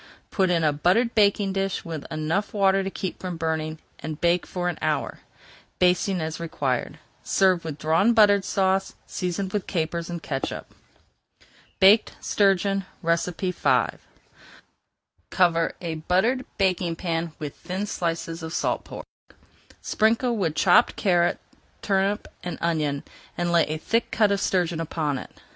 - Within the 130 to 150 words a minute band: Yes, average, 145 wpm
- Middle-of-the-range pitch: Yes, medium, 180 Hz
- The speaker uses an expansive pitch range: No, average, 3.1 semitones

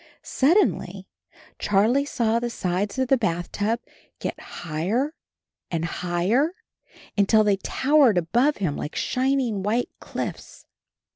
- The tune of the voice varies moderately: No, wide, 6.2 semitones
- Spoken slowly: Yes, slow, 125 wpm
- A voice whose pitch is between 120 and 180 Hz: No, high, 220 Hz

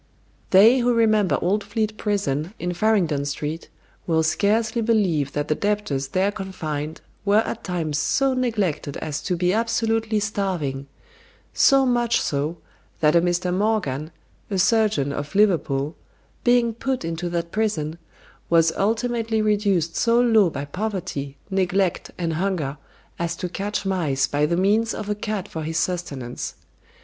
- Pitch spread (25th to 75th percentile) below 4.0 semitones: No, wide, 5.5 semitones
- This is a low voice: No, medium, 185 Hz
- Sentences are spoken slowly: No, average, 145 wpm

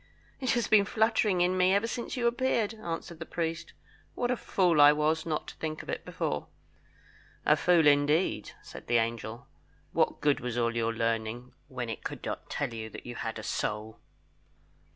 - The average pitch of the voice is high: No, medium, 155 Hz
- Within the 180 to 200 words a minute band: Yes, average, 190 wpm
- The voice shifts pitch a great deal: Yes, wide, 8.3 semitones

